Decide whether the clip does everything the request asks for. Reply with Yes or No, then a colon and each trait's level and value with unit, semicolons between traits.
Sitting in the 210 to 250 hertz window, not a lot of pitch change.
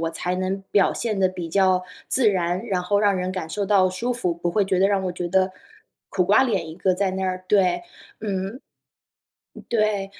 No: high, 190 Hz; narrow, 1.9 semitones